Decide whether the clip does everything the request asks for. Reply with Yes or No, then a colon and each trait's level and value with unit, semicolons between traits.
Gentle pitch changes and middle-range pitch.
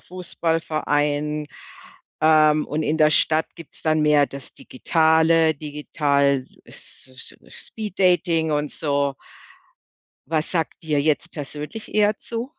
Yes: narrow, 1.8 semitones; medium, 155 Hz